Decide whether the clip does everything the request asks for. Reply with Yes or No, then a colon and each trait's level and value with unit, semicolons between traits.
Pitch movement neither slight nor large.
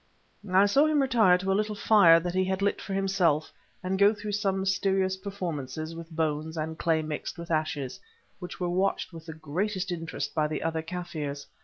Yes: average, 3.5 semitones